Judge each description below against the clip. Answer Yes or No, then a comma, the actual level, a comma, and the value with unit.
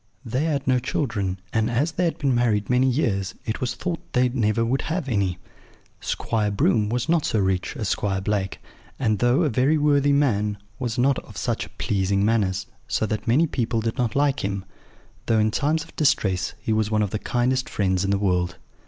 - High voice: No, low, 115 Hz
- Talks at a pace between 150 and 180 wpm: No, fast, 205 wpm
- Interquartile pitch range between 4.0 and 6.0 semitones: Yes, average, 4.7 semitones